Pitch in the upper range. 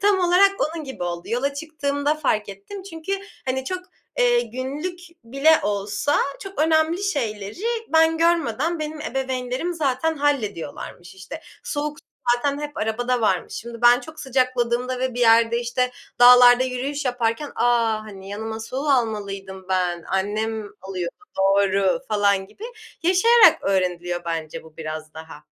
Yes: high, 245 Hz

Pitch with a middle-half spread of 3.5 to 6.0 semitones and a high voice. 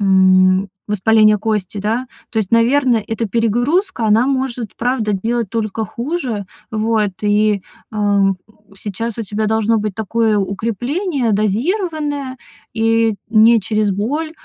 No: narrow, 2.6 semitones; high, 220 Hz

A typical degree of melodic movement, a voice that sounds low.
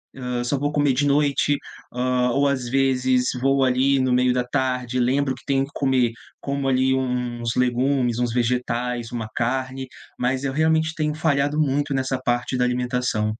No: narrow, 1.9 semitones; low, 130 Hz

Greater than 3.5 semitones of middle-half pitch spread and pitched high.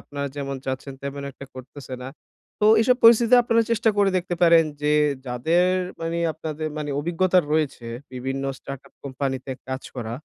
No: average, 4.8 semitones; medium, 145 Hz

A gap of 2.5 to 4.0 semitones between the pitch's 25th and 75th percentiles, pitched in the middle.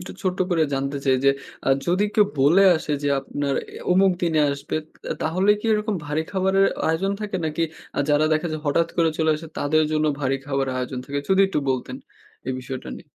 No: average, 4.8 semitones; medium, 155 Hz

